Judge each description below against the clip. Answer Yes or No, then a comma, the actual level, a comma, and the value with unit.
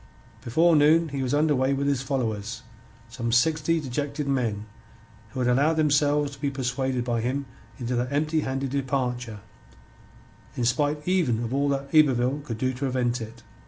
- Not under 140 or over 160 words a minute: No, average, 170 wpm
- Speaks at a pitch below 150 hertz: Yes, low, 135 Hz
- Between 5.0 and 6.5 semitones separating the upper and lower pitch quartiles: No, average, 3.0 semitones